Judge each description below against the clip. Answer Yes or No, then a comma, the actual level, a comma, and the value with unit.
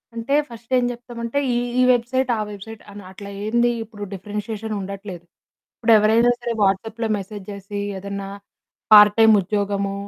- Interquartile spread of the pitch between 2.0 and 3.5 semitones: Yes, average, 2.7 semitones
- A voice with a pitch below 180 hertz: No, high, 215 Hz